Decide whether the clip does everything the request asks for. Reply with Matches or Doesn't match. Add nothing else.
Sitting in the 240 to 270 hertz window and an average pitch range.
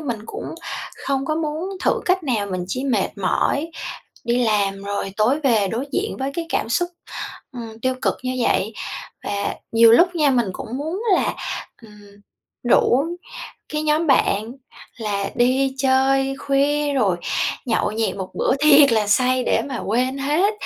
Matches